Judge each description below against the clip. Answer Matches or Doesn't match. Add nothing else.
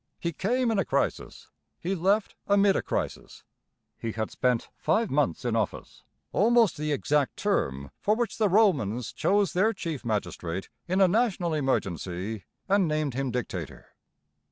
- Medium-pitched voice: Matches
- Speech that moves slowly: Doesn't match